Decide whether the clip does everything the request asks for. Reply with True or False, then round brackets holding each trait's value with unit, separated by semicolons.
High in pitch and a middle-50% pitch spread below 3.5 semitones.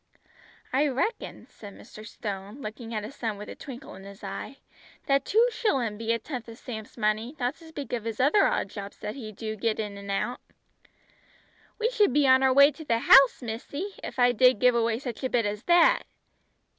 False (240 Hz; 4.3 semitones)